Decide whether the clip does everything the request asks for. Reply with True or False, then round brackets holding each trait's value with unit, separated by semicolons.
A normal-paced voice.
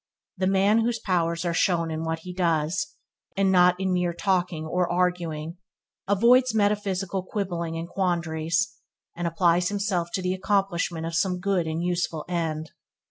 True (155 wpm)